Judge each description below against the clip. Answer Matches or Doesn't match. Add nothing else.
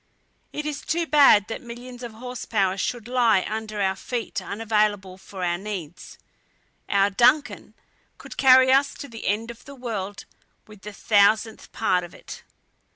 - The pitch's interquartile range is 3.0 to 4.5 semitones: Matches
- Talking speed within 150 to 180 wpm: Matches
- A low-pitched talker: Doesn't match